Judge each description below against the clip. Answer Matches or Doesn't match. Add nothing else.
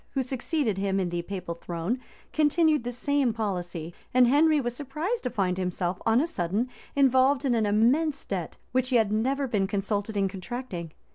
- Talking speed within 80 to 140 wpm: Doesn't match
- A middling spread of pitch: Doesn't match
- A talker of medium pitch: Doesn't match